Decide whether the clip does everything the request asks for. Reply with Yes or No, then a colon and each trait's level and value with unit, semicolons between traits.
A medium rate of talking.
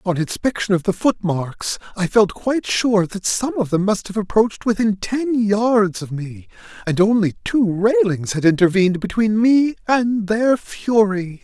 Yes: average, 170 wpm